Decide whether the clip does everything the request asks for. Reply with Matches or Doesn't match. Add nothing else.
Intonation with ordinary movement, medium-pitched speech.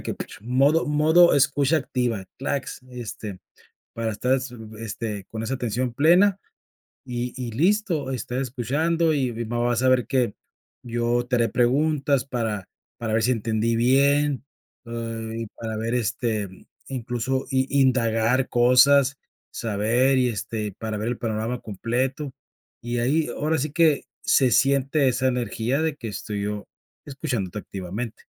Doesn't match